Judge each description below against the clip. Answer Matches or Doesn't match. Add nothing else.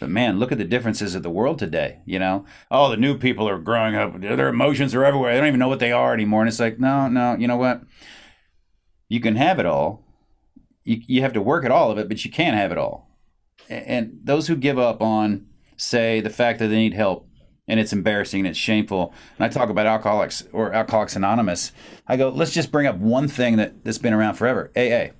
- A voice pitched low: Matches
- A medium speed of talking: Doesn't match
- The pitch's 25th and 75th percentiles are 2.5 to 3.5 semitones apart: Matches